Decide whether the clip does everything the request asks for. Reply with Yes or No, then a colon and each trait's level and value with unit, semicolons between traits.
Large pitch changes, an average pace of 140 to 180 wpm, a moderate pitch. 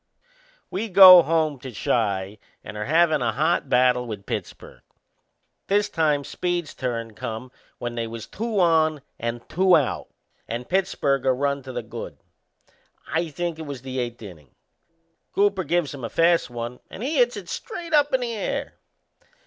Yes: wide, 6.8 semitones; average, 170 wpm; medium, 145 Hz